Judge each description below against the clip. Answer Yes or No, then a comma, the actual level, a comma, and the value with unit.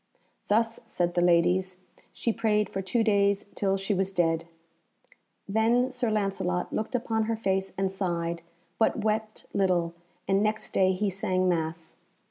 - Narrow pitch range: No, average, 3.4 semitones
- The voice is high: Yes, high, 195 Hz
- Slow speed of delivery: No, average, 150 wpm